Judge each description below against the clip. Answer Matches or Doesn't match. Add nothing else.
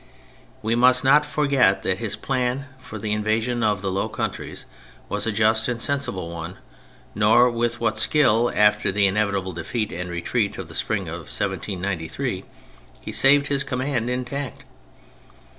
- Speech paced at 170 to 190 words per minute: Doesn't match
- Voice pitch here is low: Matches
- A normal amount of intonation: Matches